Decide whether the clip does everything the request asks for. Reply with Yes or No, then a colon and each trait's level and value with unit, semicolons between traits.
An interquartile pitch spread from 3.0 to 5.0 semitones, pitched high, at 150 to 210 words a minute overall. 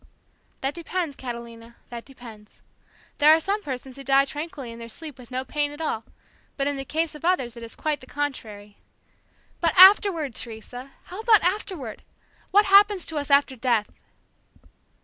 No: wide, 5.4 semitones; very high, 275 Hz; average, 170 wpm